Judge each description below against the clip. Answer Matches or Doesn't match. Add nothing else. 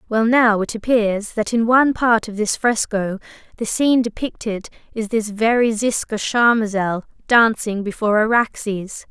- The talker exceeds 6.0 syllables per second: Doesn't match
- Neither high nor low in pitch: Doesn't match